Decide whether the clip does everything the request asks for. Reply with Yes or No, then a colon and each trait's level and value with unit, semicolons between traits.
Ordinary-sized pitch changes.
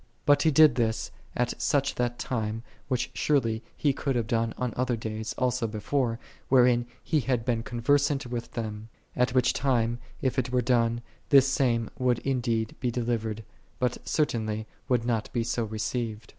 No: narrow, 2.2 semitones